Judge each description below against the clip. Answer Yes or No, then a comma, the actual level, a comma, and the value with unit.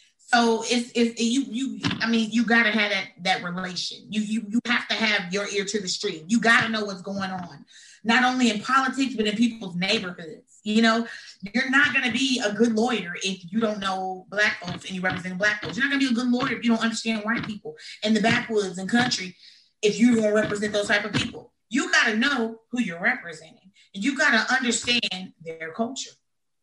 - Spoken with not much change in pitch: No, average, 3.3 semitones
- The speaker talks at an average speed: No, fast, 215 wpm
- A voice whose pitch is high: Yes, high, 220 Hz